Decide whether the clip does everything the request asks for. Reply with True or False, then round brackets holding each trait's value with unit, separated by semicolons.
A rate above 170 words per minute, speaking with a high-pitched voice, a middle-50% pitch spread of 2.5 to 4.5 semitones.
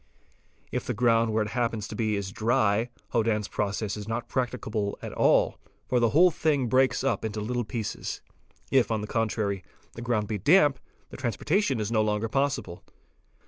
False (185 wpm; 115 Hz; 2.9 semitones)